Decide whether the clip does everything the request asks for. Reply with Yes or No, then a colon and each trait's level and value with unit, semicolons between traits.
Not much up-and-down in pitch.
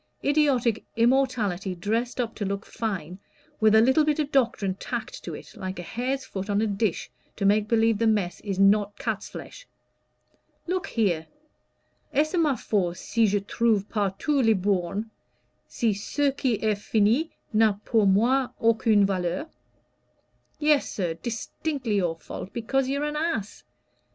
No: average, 4.8 semitones